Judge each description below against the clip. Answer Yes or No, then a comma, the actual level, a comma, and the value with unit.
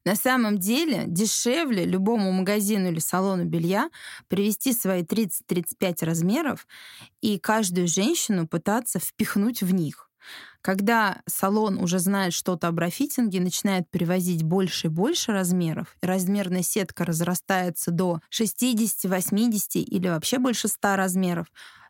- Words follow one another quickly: No, average, 120 wpm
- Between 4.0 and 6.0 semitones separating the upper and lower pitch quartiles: No, average, 3.3 semitones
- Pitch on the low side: No, high, 190 Hz